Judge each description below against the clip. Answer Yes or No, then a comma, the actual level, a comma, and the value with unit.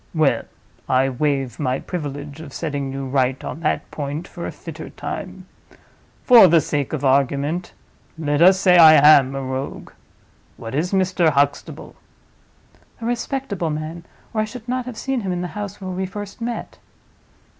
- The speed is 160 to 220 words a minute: Yes, average, 165 wpm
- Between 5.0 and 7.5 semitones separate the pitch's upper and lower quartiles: Yes, wide, 5.4 semitones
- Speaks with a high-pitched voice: No, medium, 155 Hz